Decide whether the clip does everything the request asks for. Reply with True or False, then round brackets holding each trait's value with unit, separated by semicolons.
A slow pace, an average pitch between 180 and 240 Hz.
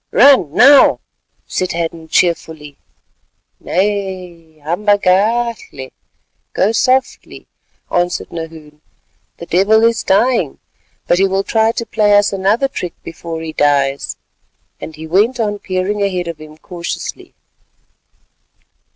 True (115 wpm; 185 Hz)